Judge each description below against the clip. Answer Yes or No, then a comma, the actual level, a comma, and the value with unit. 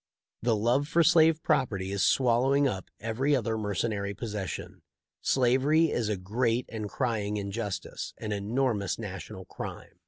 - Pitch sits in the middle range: No, low, 115 Hz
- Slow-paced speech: No, average, 145 wpm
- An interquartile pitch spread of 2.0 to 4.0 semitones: No, average, 4.5 semitones